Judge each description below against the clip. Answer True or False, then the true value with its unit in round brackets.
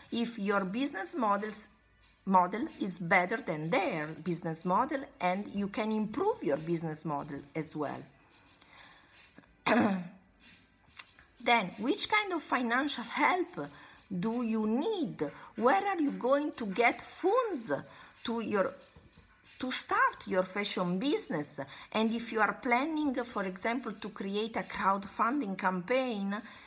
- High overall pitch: True (215 Hz)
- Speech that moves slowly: True (125 wpm)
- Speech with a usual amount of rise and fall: False (5.7 semitones)